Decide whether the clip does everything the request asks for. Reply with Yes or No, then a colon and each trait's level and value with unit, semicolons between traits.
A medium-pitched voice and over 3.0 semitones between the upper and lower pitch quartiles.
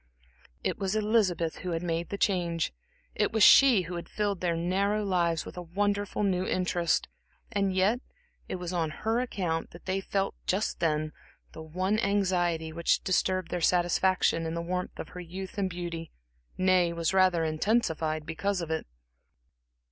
No: medium, 180 Hz; average, 2.7 semitones